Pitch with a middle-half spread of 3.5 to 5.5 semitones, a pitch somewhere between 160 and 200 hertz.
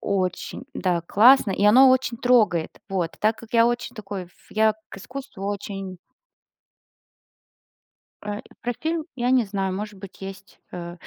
No: average, 4.0 semitones; high, 210 Hz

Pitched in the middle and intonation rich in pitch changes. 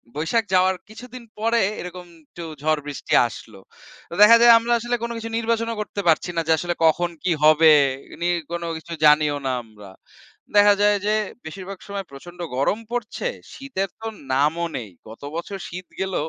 Yes: medium, 180 Hz; wide, 5.9 semitones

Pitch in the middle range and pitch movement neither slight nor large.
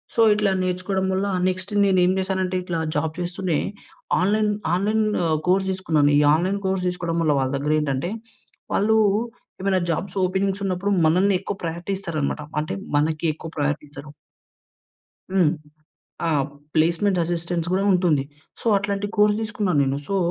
Yes: medium, 180 Hz; average, 3.7 semitones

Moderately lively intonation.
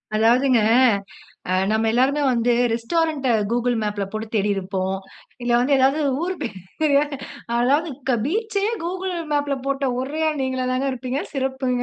Yes: average, 3.8 semitones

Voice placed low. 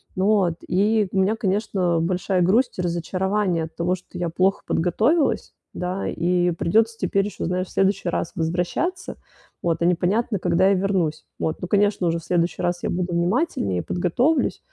No: medium, 185 Hz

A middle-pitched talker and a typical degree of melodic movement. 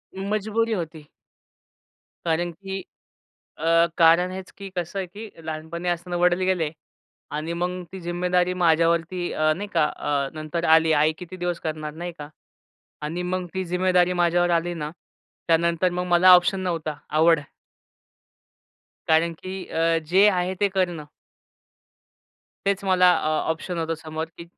No: medium, 175 Hz; narrow, 2.0 semitones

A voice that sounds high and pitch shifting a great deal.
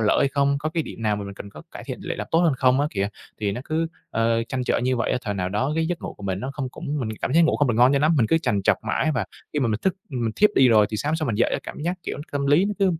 No: low, 130 Hz; wide, 5.9 semitones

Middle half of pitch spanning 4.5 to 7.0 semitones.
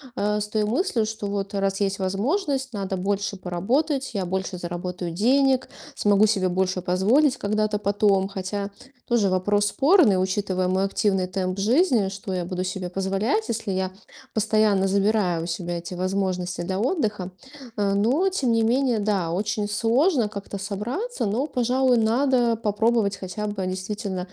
No: average, 3.4 semitones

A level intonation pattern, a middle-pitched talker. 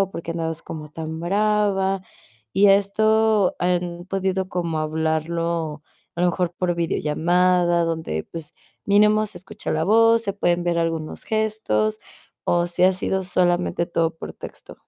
No: average, 3.1 semitones; medium, 175 Hz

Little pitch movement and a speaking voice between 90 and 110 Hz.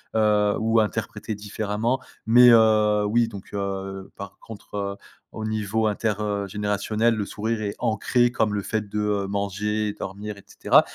Yes: narrow, 1.5 semitones; low, 105 Hz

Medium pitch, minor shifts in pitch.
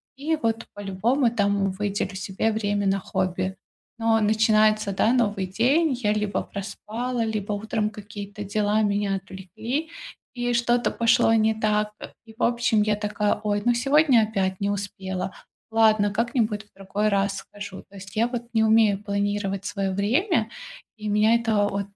No: high, 210 Hz; narrow, 2.1 semitones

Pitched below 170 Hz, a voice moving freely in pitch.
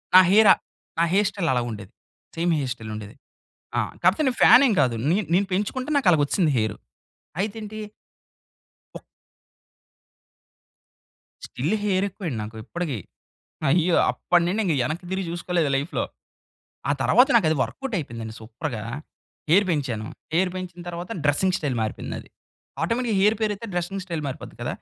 No: medium, 175 Hz; wide, 6.4 semitones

